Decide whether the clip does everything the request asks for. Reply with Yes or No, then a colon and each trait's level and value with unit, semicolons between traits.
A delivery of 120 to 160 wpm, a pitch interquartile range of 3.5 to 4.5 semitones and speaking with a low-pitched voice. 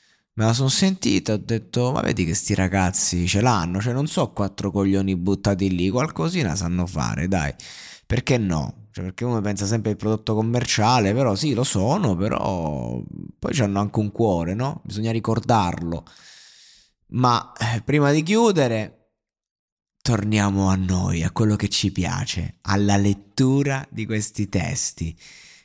Yes: average, 150 wpm; average, 4.0 semitones; low, 105 Hz